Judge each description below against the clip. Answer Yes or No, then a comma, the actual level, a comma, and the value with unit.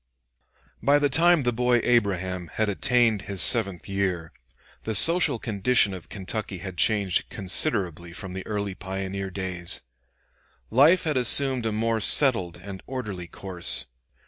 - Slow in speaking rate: No, average, 145 wpm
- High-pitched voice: No, low, 100 Hz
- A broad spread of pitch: No, average, 4.7 semitones